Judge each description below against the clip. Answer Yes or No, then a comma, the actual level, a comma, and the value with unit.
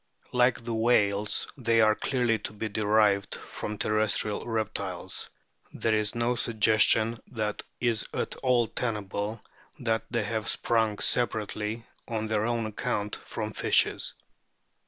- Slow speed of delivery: Yes, slow, 130 wpm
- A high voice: No, low, 110 Hz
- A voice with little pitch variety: Yes, narrow, 1.8 semitones